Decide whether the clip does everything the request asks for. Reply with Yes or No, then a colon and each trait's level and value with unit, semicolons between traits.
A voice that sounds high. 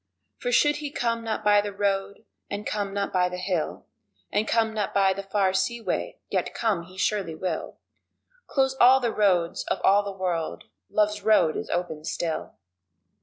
Yes: high, 200 Hz